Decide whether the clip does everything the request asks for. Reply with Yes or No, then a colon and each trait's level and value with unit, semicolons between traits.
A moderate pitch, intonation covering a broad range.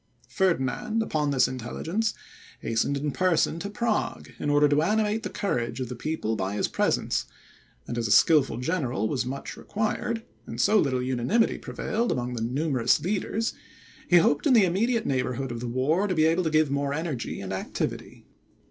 Yes: medium, 150 Hz; wide, 7.2 semitones